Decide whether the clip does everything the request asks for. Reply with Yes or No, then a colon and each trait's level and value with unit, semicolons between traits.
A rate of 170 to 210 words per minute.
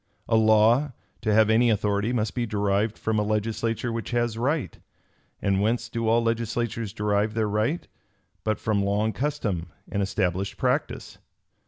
No: average, 155 wpm